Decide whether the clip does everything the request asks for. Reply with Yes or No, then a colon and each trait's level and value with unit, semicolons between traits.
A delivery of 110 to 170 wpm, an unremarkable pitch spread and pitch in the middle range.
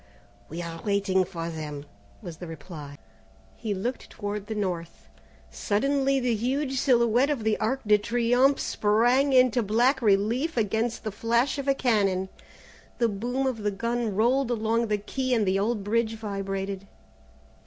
No: average, 155 wpm; average, 3.9 semitones; high, 220 Hz